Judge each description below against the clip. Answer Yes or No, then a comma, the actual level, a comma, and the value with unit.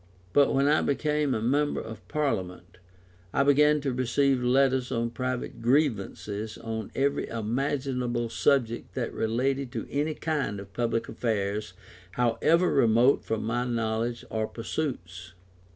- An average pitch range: Yes, average, 3.7 semitones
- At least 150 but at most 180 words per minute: No, slow, 135 wpm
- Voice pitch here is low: Yes, low, 125 Hz